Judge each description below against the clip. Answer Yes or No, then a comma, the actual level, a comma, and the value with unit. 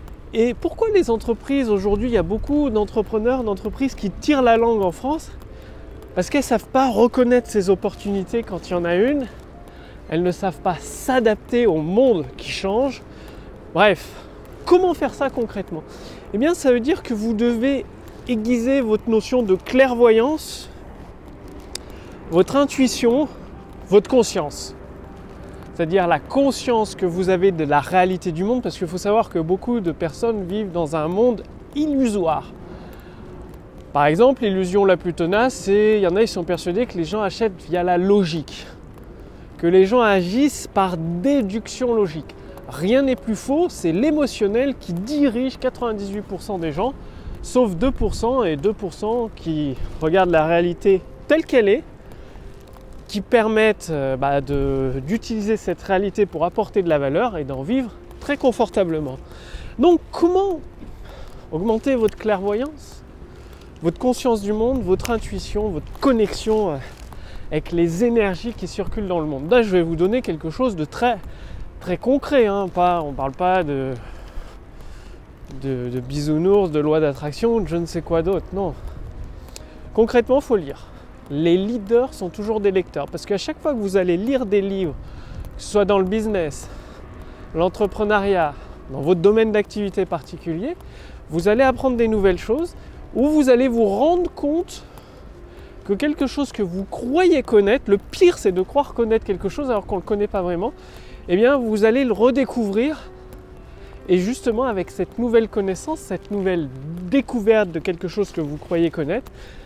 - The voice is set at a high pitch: Yes, high, 205 Hz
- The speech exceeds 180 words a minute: No, average, 160 wpm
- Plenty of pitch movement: Yes, wide, 5.7 semitones